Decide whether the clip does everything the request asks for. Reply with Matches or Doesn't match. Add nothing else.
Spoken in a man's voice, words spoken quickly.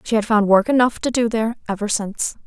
Doesn't match